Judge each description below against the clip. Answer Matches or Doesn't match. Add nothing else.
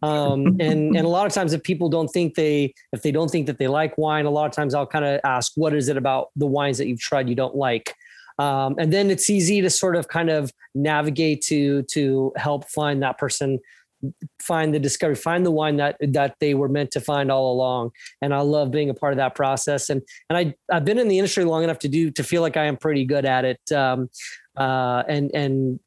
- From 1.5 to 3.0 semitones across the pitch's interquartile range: Matches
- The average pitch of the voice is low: Doesn't match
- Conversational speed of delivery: Doesn't match